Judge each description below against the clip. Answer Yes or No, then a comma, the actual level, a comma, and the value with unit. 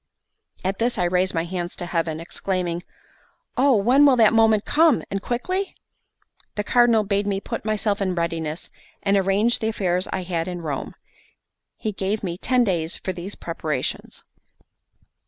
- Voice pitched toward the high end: Yes, high, 195 Hz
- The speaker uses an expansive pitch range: No, average, 4.2 semitones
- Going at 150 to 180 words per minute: Yes, average, 160 wpm